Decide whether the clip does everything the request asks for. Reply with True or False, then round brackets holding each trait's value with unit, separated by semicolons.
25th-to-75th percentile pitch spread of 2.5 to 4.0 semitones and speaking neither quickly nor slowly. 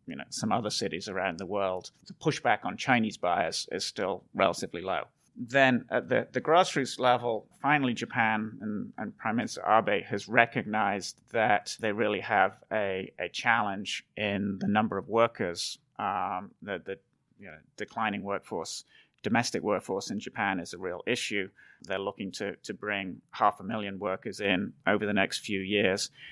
True (2.8 semitones; 170 wpm)